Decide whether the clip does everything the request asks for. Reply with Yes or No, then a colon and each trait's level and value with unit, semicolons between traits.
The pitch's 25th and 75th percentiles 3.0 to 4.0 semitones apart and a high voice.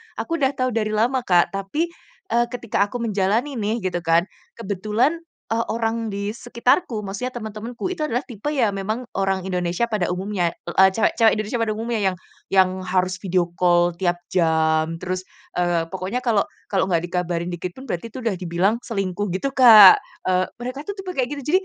No: average, 4.5 semitones; high, 205 Hz